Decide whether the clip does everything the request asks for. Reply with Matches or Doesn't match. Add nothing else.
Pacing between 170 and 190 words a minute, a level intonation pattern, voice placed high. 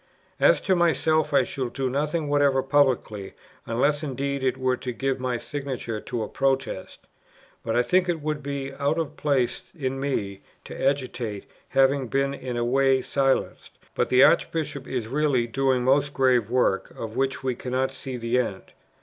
Doesn't match